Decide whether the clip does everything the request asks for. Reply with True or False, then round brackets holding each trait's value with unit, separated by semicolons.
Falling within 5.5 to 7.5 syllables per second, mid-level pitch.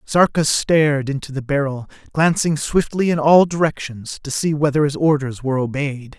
False (5.0 syllables/s; 145 Hz)